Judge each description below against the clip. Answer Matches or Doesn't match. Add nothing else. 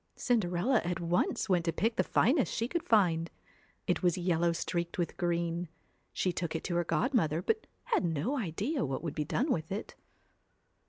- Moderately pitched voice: Matches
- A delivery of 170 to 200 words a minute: Matches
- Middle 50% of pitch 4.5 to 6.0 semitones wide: Matches